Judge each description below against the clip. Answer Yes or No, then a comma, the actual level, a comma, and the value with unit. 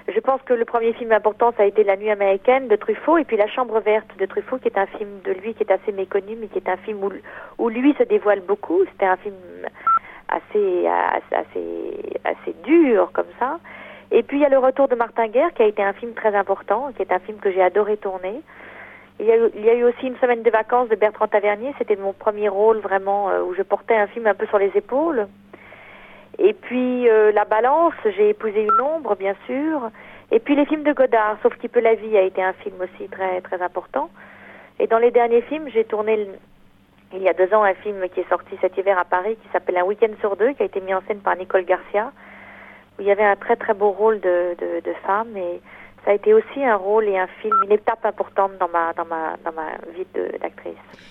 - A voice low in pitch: No, high, 215 Hz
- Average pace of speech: No, fast, 245 wpm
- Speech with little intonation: No, average, 4.2 semitones